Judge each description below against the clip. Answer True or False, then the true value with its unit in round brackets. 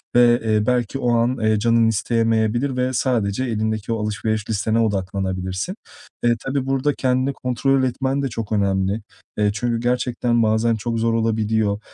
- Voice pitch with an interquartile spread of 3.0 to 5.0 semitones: False (2.6 semitones)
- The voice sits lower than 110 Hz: False (115 Hz)